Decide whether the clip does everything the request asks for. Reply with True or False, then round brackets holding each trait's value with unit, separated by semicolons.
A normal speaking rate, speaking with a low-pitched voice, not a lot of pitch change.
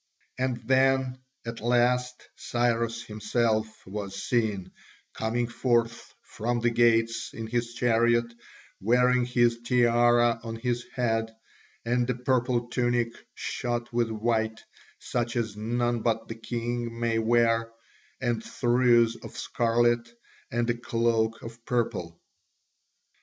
False (120 wpm; 120 Hz; 1.1 semitones)